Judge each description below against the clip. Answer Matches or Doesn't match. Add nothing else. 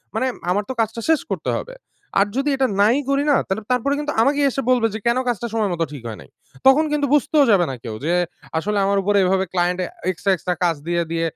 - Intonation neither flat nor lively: Doesn't match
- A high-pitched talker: Matches